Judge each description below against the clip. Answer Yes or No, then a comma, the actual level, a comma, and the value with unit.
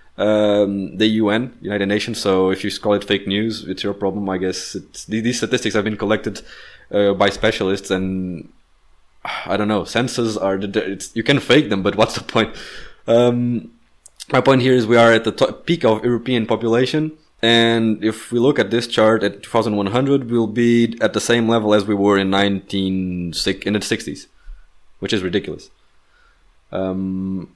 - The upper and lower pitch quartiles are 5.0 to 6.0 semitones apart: No, average, 3.0 semitones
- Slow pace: No, average, 180 wpm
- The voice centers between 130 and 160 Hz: No, low, 105 Hz